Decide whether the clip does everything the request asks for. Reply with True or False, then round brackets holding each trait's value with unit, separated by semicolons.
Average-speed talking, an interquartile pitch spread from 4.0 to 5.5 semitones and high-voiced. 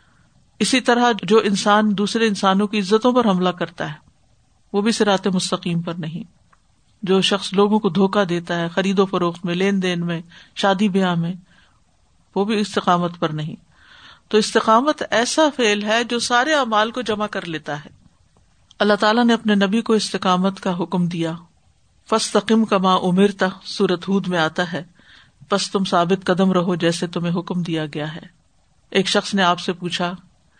False (175 wpm; 3.2 semitones; 195 Hz)